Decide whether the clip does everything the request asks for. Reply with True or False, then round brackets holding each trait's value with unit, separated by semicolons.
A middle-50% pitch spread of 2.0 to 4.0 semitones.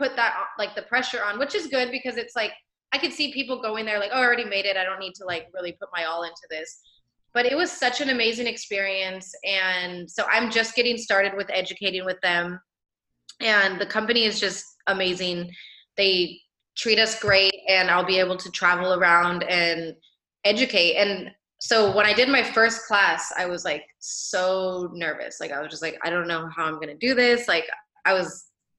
False (4.5 semitones)